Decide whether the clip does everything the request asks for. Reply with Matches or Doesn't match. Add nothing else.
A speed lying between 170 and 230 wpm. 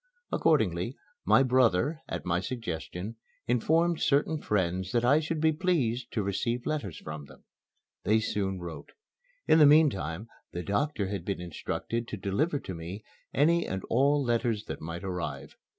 Doesn't match